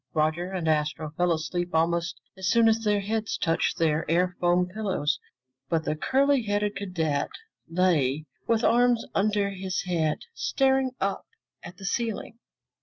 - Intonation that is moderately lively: Yes, average, 4.6 semitones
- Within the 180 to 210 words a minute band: No, average, 150 wpm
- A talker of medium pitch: Yes, medium, 180 Hz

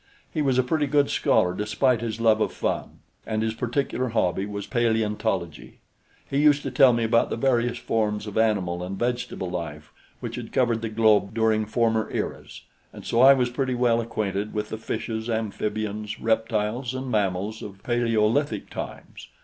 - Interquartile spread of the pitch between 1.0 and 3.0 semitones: Yes, narrow, 2.6 semitones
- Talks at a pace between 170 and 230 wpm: Yes, average, 175 wpm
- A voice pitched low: Yes, low, 110 Hz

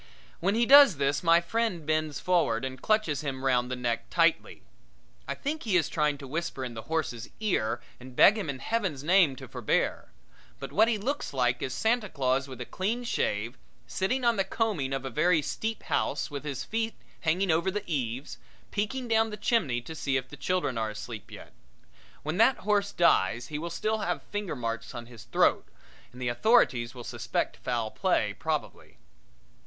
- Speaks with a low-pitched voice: No, medium, 155 Hz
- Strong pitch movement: Yes, wide, 8.4 semitones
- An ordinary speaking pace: Yes, average, 190 wpm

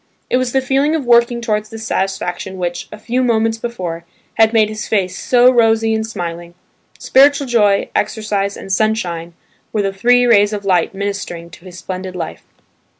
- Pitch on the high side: Yes, high, 215 Hz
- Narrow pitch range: No, average, 4.1 semitones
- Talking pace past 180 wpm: No, average, 175 wpm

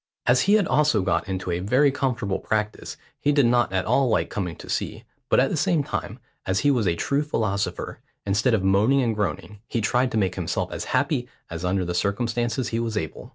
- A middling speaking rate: No, fast, 220 wpm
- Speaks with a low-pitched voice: Yes, low, 110 Hz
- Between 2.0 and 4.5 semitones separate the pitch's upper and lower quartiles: No, average, 5.0 semitones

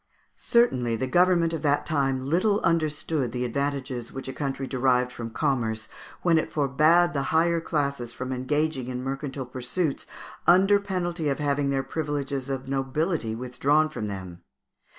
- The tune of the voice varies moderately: Yes, average, 3.7 semitones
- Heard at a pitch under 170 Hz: Yes, medium, 140 Hz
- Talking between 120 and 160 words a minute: Yes, average, 150 wpm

